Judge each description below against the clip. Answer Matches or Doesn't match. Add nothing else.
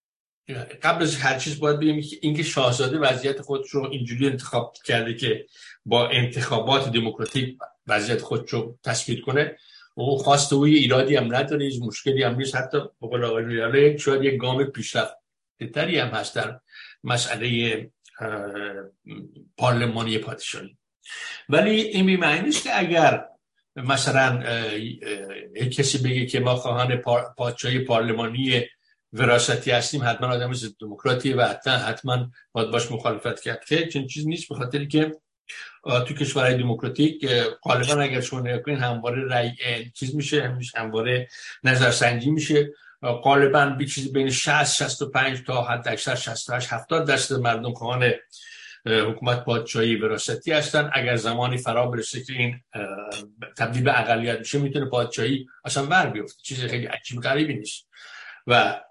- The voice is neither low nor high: Doesn't match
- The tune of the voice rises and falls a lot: Doesn't match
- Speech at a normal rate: Matches